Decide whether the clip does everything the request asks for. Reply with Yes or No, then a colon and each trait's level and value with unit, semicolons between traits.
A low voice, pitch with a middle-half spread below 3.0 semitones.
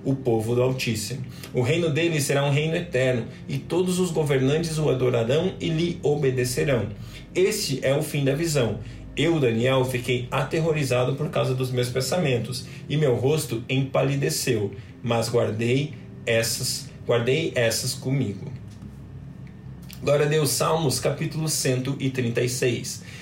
No: low, 130 Hz; average, 3.3 semitones